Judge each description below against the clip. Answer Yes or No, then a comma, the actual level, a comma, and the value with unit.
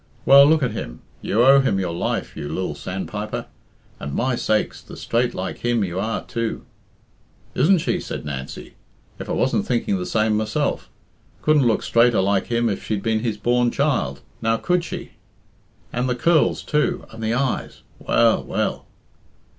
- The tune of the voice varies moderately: Yes, average, 3.7 semitones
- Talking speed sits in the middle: Yes, average, 170 wpm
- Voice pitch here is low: Yes, low, 115 Hz